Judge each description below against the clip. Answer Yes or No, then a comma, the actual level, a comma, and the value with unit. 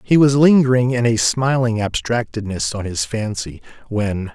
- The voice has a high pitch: No, low, 115 Hz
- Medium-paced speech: Yes, average, 150 wpm